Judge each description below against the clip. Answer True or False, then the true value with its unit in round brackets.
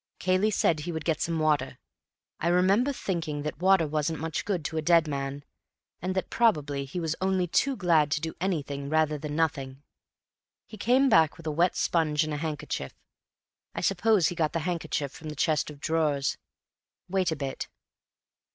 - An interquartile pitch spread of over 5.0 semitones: False (3.2 semitones)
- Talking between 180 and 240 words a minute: True (185 wpm)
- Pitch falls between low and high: True (160 Hz)